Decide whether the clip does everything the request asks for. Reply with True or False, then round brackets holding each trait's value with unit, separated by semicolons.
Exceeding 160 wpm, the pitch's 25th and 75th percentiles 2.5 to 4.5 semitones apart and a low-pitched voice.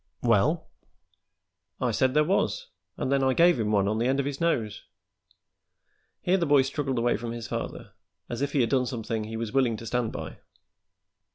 True (195 wpm; 3.8 semitones; 130 Hz)